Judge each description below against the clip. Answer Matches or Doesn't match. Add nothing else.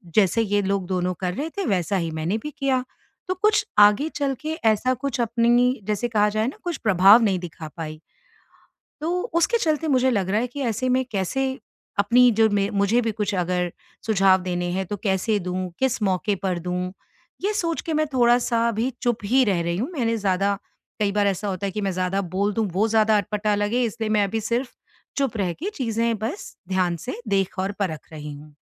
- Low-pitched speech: Doesn't match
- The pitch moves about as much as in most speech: Matches